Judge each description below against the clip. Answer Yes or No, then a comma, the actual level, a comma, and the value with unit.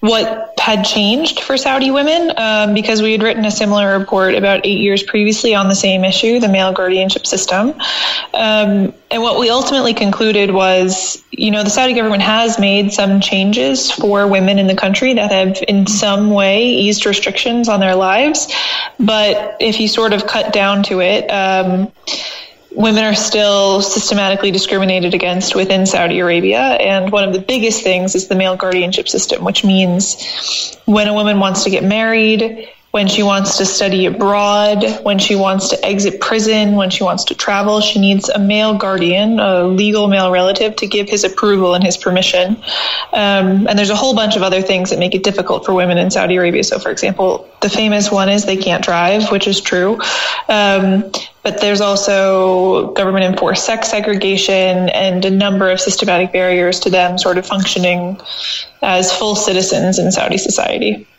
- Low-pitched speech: No, high, 200 Hz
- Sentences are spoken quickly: No, average, 180 wpm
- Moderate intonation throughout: No, narrow, 2.2 semitones